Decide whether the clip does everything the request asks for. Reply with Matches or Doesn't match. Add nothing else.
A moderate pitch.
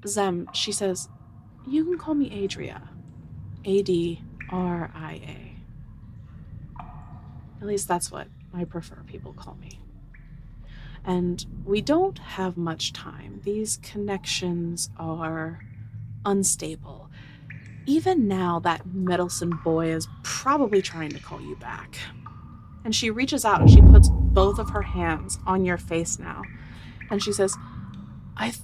Matches